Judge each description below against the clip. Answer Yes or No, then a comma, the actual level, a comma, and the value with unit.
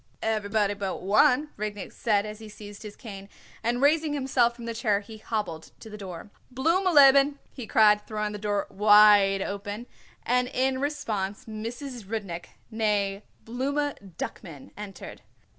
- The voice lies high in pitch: Yes, high, 215 Hz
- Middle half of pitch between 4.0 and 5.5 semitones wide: No, average, 3.6 semitones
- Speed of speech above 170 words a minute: No, average, 150 wpm